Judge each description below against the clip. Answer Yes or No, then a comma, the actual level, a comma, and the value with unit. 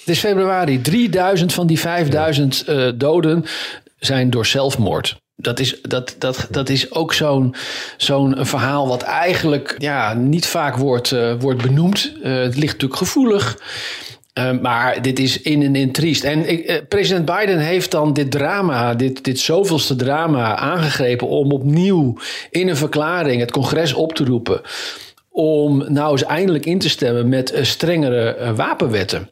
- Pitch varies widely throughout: No, average, 4.3 semitones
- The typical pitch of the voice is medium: Yes, medium, 145 Hz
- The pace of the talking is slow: No, average, 170 wpm